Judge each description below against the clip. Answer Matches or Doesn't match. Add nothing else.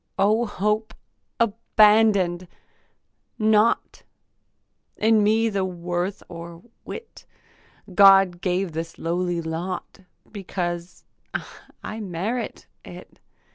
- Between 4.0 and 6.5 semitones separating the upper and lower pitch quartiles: Doesn't match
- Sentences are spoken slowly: Matches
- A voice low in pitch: Doesn't match